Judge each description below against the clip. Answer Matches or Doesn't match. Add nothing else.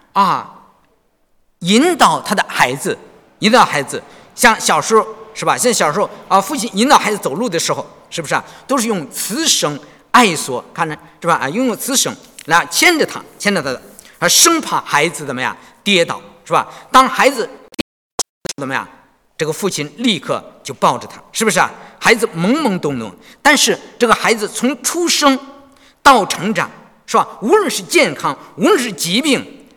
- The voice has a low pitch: Doesn't match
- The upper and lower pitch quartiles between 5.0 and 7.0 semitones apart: Matches